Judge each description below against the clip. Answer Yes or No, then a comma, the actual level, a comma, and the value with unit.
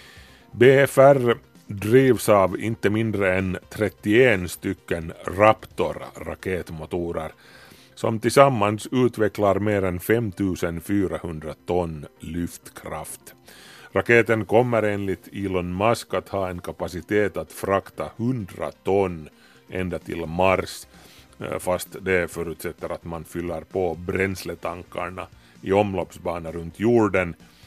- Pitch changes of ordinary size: Yes, average, 3.7 semitones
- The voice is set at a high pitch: No, very low, 95 Hz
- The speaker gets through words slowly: Yes, slow, 100 wpm